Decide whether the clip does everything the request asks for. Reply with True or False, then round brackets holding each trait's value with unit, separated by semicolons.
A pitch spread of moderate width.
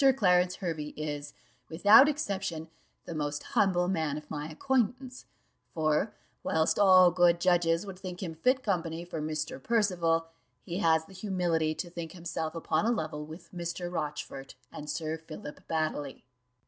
True (3.0 semitones)